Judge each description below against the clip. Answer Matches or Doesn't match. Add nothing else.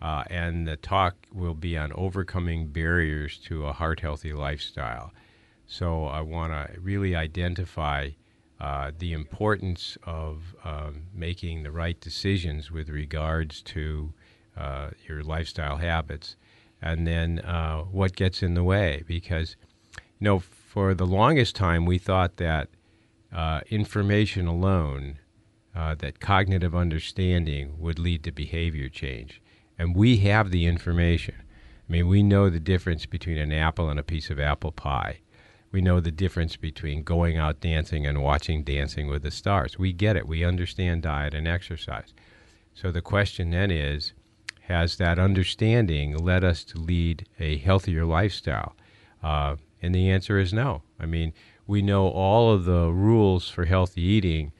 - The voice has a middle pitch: Doesn't match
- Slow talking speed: Doesn't match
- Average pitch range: Matches